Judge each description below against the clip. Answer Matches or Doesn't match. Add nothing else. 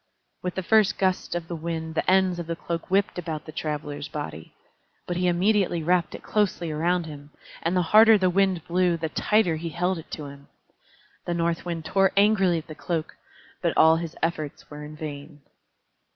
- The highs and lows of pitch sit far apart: Doesn't match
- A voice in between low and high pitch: Matches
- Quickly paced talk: Doesn't match